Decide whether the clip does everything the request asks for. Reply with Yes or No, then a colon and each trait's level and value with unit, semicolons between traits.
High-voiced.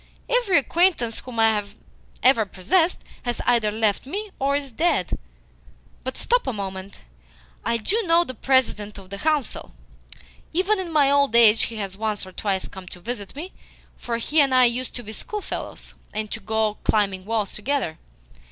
Yes: high, 235 Hz